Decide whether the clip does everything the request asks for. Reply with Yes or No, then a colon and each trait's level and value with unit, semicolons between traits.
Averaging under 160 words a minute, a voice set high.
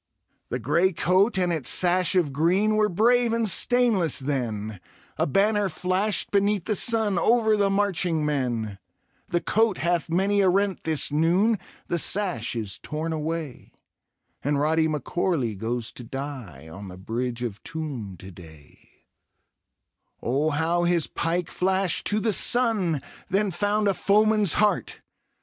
No: average, 150 wpm; medium, 170 Hz